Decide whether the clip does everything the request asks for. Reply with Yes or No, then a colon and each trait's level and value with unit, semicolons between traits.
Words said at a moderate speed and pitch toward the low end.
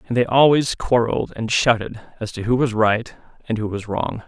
No: fast, 210 wpm; low, 115 Hz